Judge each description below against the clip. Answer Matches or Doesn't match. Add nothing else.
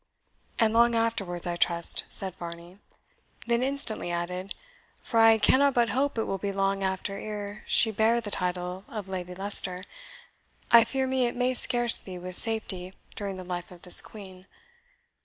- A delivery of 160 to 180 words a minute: Matches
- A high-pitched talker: Matches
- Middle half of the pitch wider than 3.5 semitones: Matches